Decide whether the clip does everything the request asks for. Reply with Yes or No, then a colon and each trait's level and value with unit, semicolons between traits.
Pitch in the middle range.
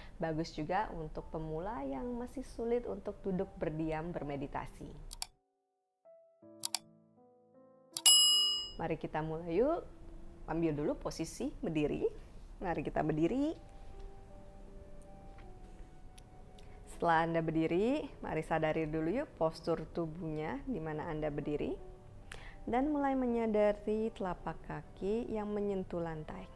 Yes: medium, 165 Hz